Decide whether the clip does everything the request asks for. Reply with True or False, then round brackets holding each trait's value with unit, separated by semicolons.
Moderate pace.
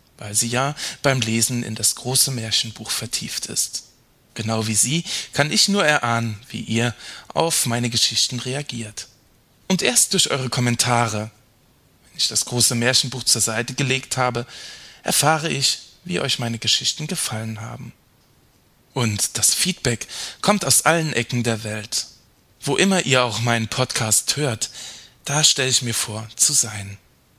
True (150 wpm)